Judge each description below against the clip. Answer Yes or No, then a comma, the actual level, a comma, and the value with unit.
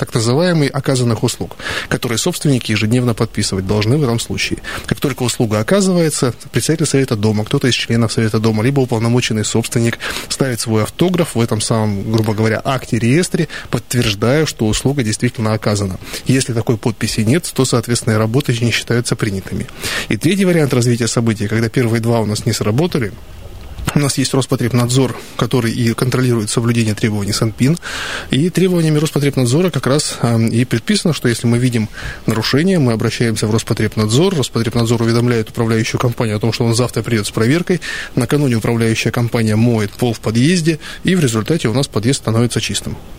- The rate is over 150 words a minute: Yes, fast, 160 wpm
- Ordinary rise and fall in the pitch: Yes, average, 3.3 semitones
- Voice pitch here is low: Yes, low, 120 Hz